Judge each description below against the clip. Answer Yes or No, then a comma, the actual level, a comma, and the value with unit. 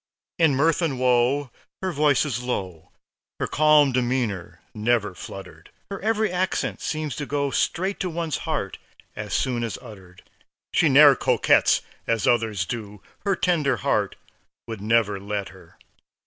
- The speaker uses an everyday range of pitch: No, wide, 6.2 semitones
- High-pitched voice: No, low, 130 Hz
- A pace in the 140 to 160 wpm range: Yes, average, 150 wpm